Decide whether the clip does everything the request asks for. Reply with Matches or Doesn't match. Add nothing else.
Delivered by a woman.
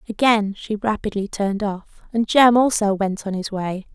Matches